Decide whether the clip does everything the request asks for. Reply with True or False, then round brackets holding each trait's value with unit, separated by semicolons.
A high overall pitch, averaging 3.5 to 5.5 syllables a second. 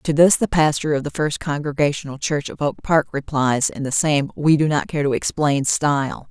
False (150 Hz; 5.0 syllables/s)